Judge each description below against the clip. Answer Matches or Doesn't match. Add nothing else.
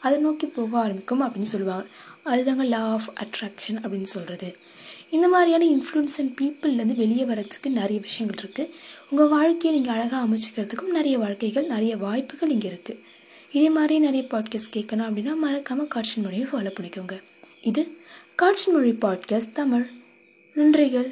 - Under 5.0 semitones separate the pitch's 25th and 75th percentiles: Doesn't match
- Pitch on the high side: Matches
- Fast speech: Matches